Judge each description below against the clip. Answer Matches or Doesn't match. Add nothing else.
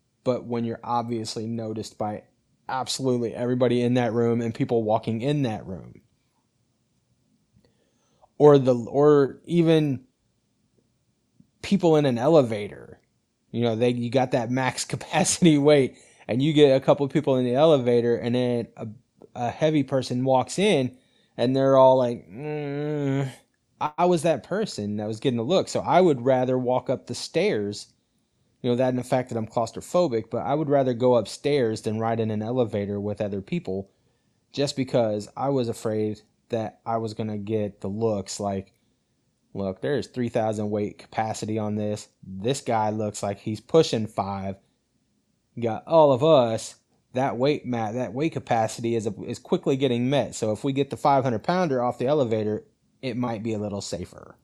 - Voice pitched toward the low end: Matches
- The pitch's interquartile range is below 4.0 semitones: Matches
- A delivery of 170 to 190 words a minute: Matches